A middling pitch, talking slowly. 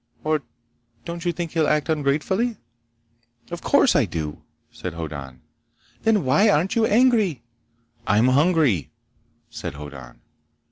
Yes: medium, 150 Hz; slow, 125 wpm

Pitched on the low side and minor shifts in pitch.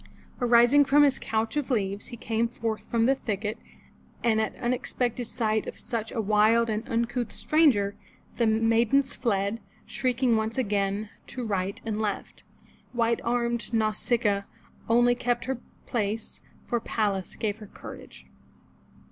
No: high, 230 Hz; narrow, 2.1 semitones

